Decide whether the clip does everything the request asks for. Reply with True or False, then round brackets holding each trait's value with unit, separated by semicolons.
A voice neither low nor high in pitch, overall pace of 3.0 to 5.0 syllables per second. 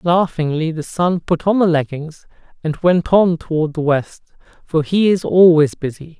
True (165 Hz; 4.5 syllables/s)